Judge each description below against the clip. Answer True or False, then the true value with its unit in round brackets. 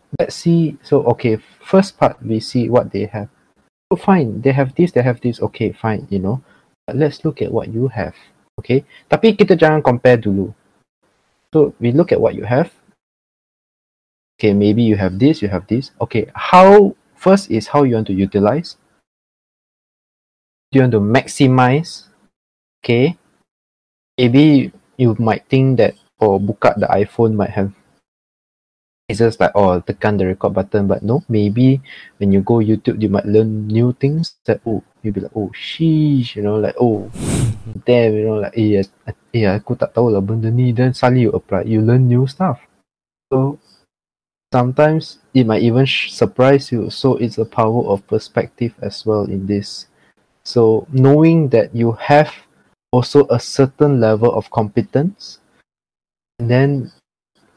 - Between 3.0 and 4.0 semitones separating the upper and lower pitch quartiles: False (4.4 semitones)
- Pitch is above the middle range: False (120 Hz)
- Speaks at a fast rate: True (160 wpm)